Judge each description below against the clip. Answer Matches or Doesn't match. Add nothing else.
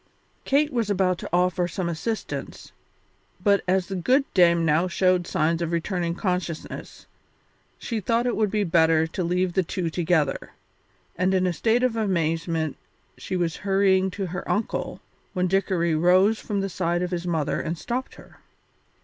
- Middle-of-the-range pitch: Matches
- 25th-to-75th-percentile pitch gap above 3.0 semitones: Doesn't match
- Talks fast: Doesn't match